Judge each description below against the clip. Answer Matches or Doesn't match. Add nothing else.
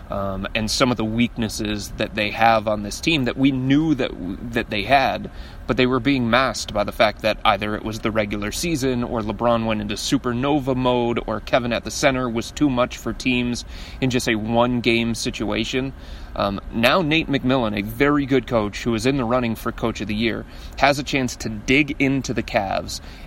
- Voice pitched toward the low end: Matches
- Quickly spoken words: Matches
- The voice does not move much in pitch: Doesn't match